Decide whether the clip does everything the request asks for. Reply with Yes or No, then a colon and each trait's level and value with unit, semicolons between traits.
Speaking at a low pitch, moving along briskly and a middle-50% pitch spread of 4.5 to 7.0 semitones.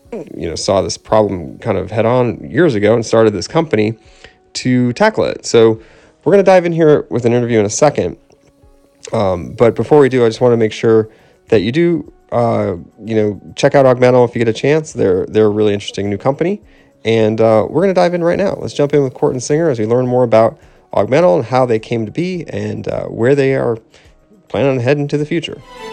Yes: low, 120 Hz; fast, 235 wpm; average, 5.1 semitones